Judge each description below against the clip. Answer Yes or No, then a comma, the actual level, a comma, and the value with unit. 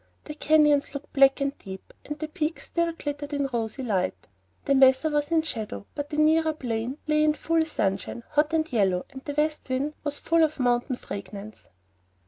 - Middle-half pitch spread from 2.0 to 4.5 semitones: Yes, average, 4.0 semitones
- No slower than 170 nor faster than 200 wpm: Yes, average, 190 wpm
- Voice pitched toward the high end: Yes, very high, 290 Hz